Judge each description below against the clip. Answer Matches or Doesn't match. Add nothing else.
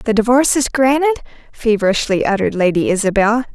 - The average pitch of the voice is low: Doesn't match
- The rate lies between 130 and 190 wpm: Matches